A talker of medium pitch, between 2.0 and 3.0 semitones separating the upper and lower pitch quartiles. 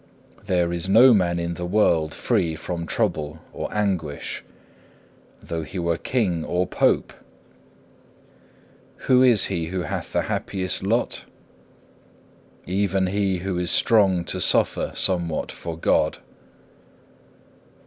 No: very low, 90 Hz; average, 2.7 semitones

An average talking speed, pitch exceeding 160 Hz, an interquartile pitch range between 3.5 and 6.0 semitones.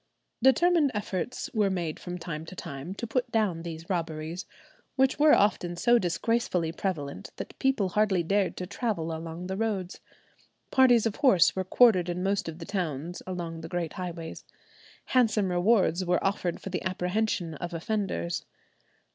Yes: average, 160 wpm; medium, 185 Hz; average, 4.1 semitones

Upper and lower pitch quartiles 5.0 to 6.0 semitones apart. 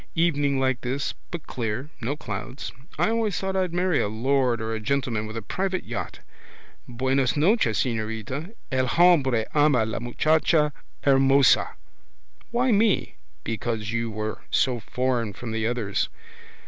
Yes: wide, 5.4 semitones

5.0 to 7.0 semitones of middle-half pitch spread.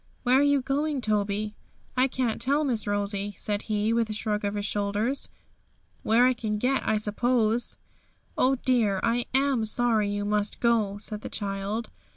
No: average, 3.3 semitones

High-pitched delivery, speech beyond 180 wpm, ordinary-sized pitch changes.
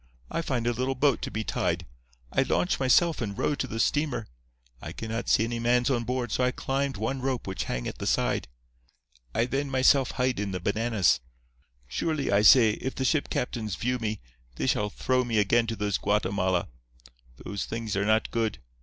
No: low, 115 Hz; average, 200 wpm; average, 3.7 semitones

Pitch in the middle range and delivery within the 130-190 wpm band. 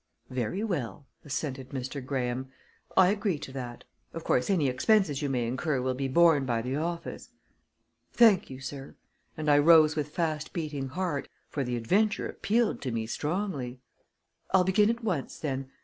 Yes: medium, 145 Hz; average, 165 wpm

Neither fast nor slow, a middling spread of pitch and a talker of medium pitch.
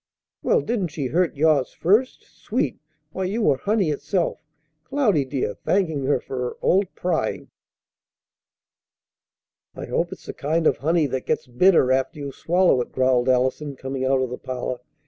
No: average, 165 wpm; wide, 5.8 semitones; medium, 145 Hz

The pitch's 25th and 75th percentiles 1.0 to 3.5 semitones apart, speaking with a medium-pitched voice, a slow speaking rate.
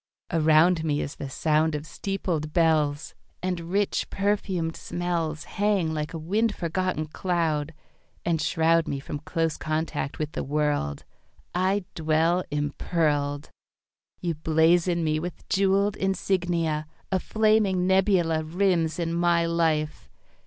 Yes: average, 2.8 semitones; medium, 165 Hz; slow, 125 wpm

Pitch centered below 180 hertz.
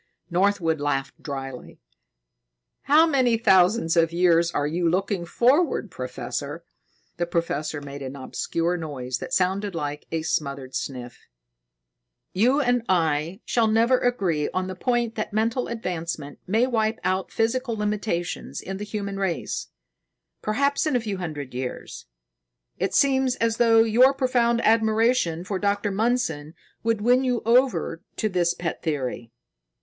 No: high, 190 Hz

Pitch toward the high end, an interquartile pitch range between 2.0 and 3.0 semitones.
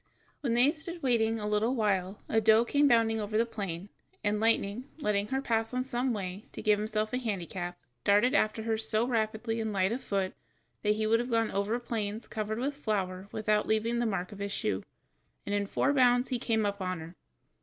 Yes: high, 220 Hz; average, 2.7 semitones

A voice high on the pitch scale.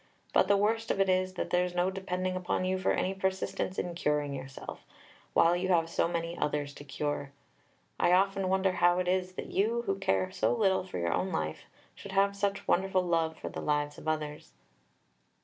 No: medium, 180 Hz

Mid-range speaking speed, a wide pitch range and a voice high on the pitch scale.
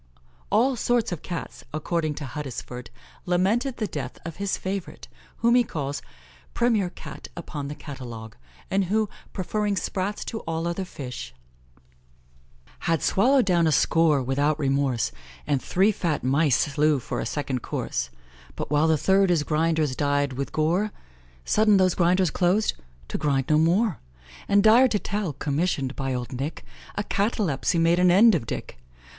No: average, 160 wpm; wide, 5.7 semitones; medium, 165 Hz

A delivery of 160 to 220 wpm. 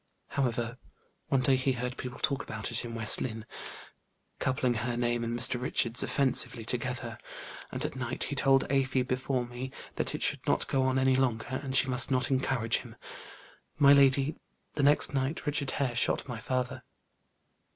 Yes: average, 175 wpm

